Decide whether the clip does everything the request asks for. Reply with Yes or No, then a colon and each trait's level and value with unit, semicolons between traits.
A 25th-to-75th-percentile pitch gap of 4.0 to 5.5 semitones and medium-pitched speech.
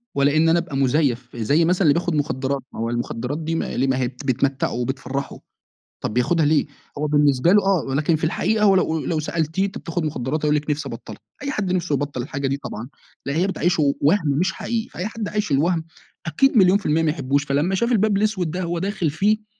Yes: average, 4.9 semitones; medium, 155 Hz